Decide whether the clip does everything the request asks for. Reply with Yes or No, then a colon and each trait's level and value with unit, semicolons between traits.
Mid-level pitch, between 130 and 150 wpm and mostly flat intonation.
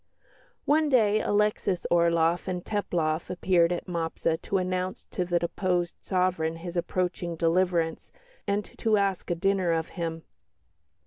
Yes: medium, 180 Hz; slow, 135 wpm; narrow, 2.3 semitones